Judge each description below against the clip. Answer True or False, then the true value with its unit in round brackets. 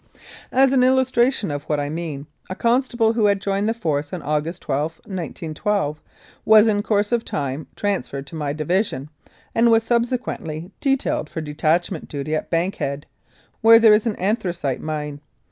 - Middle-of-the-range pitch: True (180 Hz)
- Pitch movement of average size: False (7.0 semitones)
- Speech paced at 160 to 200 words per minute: True (165 wpm)